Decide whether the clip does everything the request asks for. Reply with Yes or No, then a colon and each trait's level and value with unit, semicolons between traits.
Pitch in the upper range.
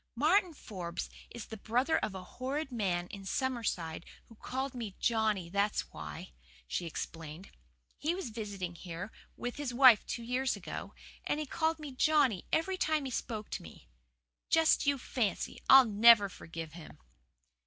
Yes: high, 230 Hz